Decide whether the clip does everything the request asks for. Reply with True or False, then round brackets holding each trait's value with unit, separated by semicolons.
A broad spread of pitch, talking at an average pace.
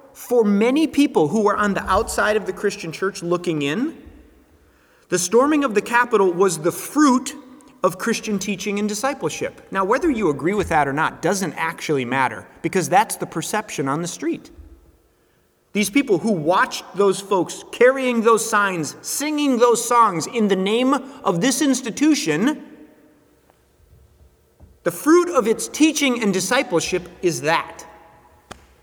True (6.1 semitones; 150 wpm)